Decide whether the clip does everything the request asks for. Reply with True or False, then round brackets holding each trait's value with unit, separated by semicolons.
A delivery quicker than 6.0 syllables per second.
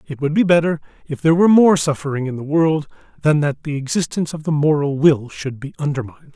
True (6.3 syllables/s)